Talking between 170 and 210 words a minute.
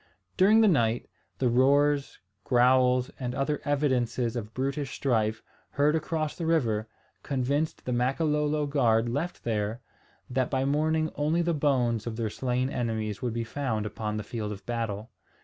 No: average, 155 wpm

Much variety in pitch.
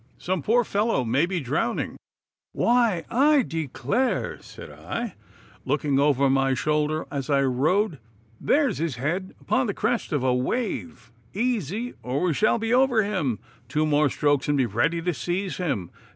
Yes: wide, 8.0 semitones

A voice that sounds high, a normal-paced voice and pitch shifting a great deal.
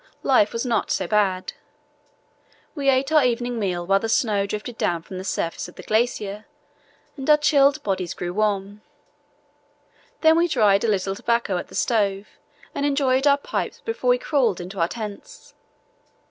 Yes: high, 220 Hz; average, 170 wpm; wide, 5.7 semitones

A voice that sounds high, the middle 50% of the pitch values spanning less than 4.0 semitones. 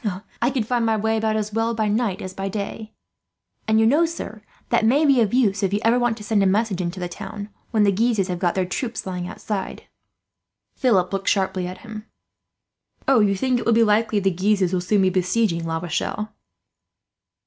Yes: high, 210 Hz; average, 3.1 semitones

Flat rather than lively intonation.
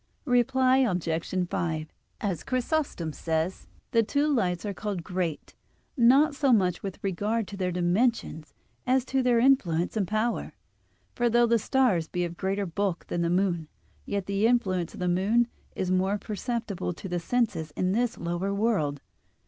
No: average, 5.3 semitones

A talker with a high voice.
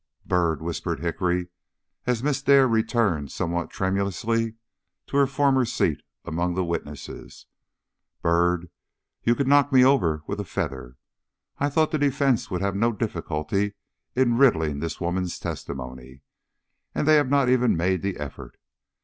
No: very low, 95 Hz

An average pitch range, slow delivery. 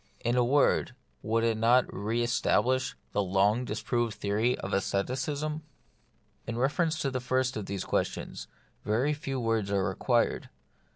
No: average, 3.3 semitones; average, 150 wpm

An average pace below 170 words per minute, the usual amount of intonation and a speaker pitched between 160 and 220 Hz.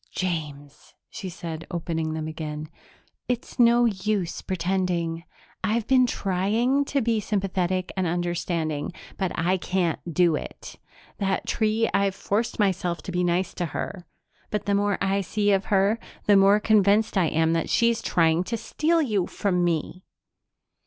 Yes: average, 150 wpm; average, 3.6 semitones; high, 190 Hz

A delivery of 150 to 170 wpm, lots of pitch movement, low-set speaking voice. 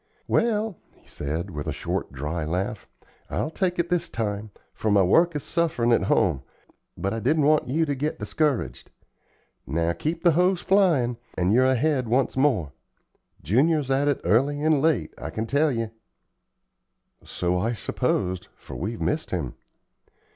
Yes: average, 160 wpm; wide, 8.5 semitones; low, 130 Hz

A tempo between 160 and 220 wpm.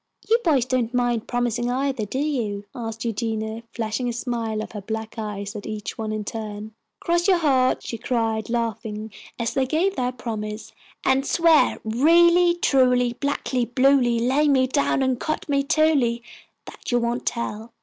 Yes: average, 170 wpm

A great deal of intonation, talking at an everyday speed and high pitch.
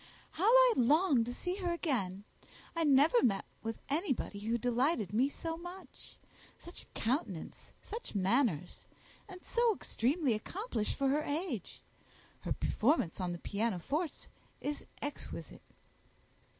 No: wide, 7.5 semitones; slow, 130 wpm; very high, 275 Hz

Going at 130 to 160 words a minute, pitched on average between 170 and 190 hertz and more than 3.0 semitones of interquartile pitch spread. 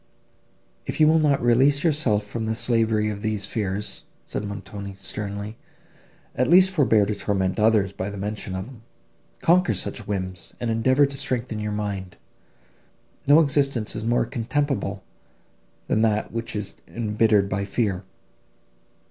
No: average, 150 wpm; low, 110 Hz; average, 3.9 semitones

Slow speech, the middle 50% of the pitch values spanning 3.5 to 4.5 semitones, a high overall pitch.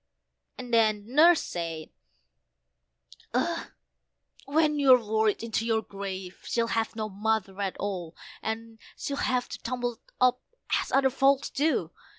Yes: slow, 130 wpm; average, 3.8 semitones; high, 225 Hz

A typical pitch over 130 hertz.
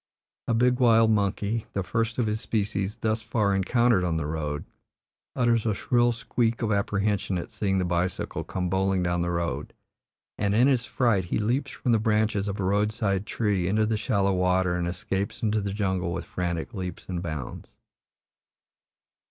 No: low, 100 Hz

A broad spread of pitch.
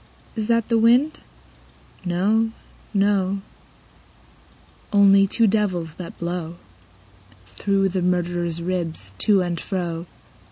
No: average, 3.1 semitones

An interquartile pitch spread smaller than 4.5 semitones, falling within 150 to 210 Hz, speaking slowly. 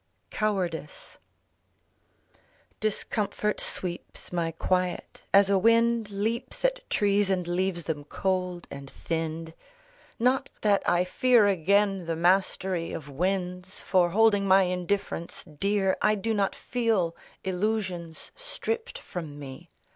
Yes: average, 3.2 semitones; high, 190 Hz; slow, 115 wpm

